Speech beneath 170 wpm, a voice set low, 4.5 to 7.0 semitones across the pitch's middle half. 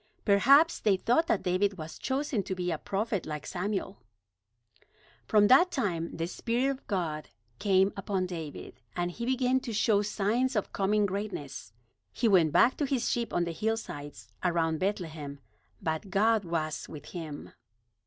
No: average, 160 wpm; high, 195 Hz; average, 5.3 semitones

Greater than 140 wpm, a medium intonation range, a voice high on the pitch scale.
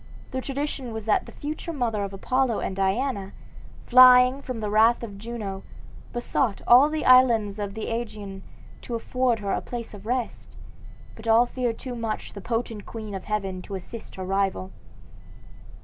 Yes: average, 170 wpm; average, 3.8 semitones; high, 225 Hz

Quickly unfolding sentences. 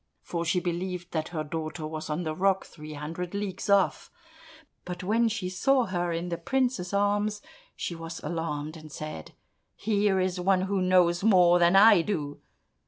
No: average, 170 wpm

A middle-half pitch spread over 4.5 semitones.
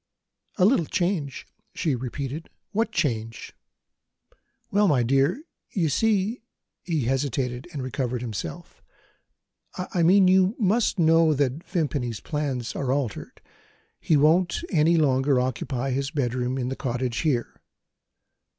Yes: average, 5.3 semitones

